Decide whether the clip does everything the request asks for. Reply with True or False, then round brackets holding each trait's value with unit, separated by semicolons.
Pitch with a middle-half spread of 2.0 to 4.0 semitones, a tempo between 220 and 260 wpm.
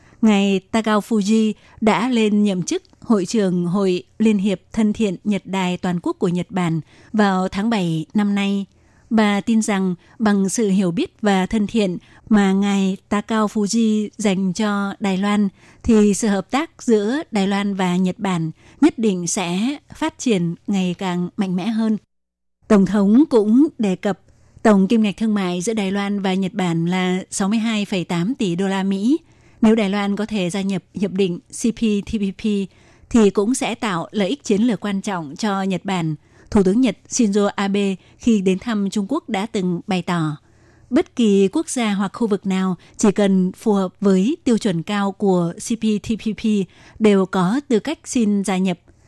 False (2.7 semitones; 180 wpm)